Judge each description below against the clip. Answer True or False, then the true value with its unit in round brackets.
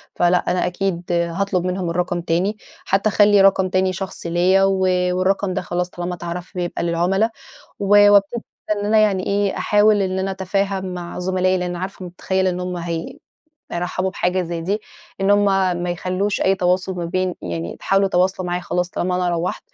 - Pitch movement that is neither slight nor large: False (1.6 semitones)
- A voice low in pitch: False (185 Hz)